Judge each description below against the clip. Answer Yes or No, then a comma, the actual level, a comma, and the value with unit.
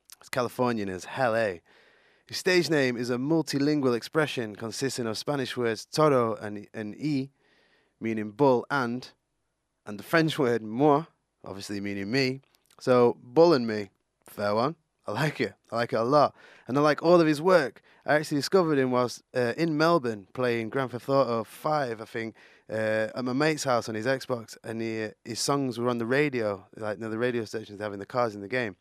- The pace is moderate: Yes, average, 195 wpm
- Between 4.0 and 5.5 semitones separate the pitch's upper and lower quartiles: Yes, average, 4.5 semitones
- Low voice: Yes, low, 125 Hz